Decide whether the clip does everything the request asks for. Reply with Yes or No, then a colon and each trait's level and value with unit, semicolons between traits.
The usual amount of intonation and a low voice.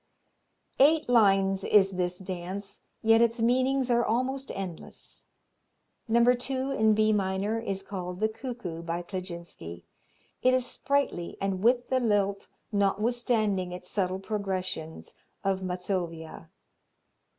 No: average, 4.4 semitones; high, 200 Hz